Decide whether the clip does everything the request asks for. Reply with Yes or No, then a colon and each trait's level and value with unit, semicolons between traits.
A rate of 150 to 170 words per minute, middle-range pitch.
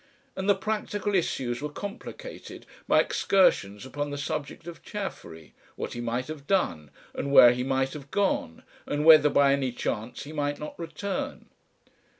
Yes: average, 160 wpm; medium, 145 Hz